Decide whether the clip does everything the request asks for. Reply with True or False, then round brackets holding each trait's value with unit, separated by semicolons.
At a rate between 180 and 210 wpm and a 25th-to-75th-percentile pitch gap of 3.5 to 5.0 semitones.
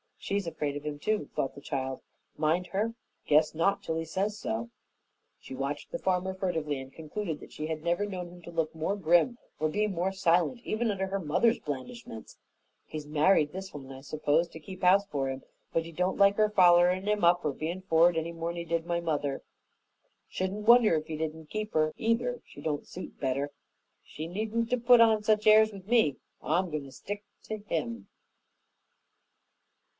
True (195 wpm; 4.7 semitones)